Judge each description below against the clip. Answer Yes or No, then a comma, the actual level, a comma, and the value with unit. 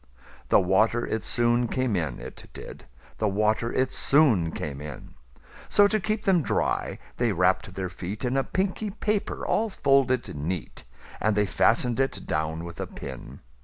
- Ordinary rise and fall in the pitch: No, wide, 7.5 semitones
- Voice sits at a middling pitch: No, low, 110 Hz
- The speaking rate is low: No, average, 150 wpm